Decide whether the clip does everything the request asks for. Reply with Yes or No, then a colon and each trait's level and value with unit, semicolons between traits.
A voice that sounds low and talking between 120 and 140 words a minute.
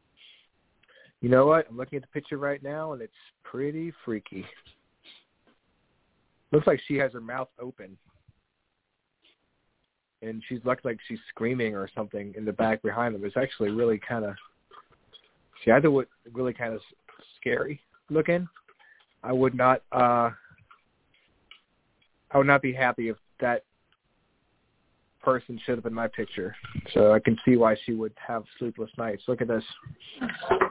No: low, 125 Hz; average, 150 wpm